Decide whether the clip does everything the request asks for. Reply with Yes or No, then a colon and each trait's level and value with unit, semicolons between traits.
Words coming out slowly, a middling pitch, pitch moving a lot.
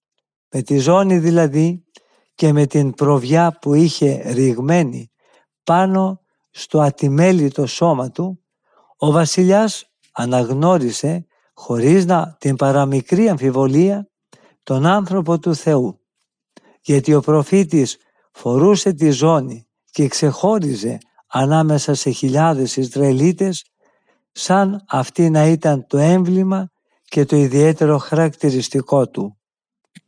No: slow, 100 wpm; medium, 155 Hz; average, 4.1 semitones